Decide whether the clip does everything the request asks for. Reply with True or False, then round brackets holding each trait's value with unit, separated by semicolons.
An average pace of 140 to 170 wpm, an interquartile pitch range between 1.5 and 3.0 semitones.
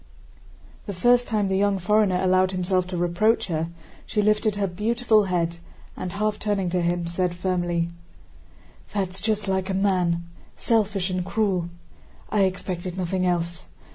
True (145 wpm; 2.7 semitones)